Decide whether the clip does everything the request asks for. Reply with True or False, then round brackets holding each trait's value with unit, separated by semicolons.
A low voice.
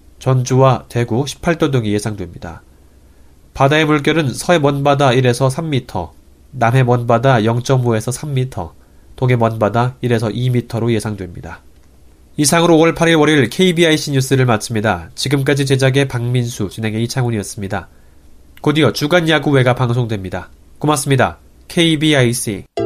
True (120 Hz)